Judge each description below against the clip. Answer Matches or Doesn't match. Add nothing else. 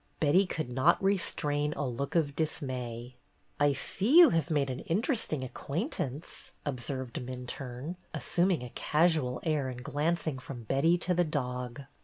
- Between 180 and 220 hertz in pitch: Doesn't match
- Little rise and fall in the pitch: Doesn't match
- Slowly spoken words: Doesn't match